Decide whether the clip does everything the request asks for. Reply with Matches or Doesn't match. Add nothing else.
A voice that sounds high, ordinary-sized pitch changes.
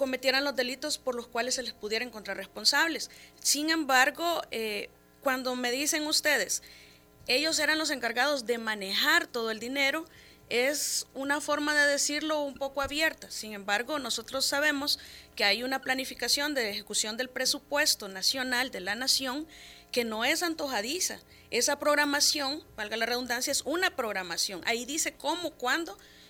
Matches